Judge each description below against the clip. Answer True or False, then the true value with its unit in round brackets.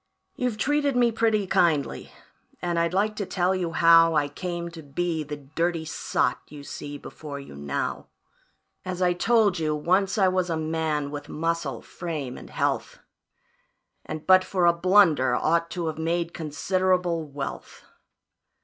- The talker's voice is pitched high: False (170 Hz)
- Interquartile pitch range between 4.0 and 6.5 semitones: False (3.4 semitones)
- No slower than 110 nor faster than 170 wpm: True (160 wpm)